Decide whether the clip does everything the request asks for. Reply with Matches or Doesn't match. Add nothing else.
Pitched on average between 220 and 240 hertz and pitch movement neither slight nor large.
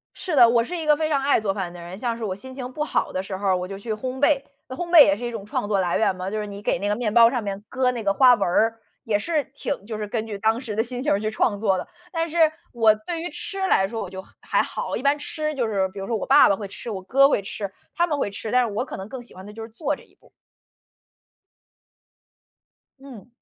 Matches